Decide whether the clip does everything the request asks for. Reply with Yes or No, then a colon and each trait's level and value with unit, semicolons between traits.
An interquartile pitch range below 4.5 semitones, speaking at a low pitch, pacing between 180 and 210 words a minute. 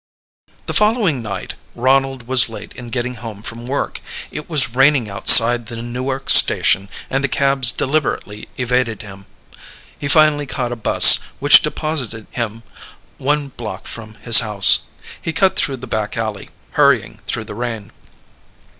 No: average, 3.5 semitones; low, 125 Hz; average, 150 wpm